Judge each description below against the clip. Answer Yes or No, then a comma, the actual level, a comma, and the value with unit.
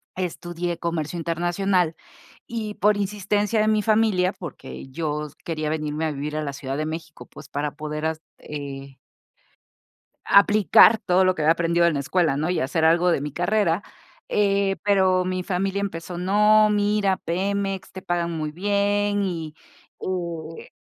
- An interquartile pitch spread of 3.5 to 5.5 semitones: Yes, average, 4.2 semitones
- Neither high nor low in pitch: Yes, medium, 175 Hz